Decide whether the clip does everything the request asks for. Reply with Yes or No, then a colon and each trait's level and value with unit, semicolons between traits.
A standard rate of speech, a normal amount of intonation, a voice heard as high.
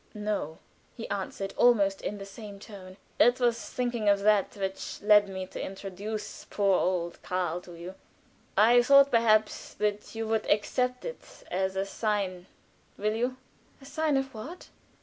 Yes: average, 160 wpm; average, 3.4 semitones; high, 210 Hz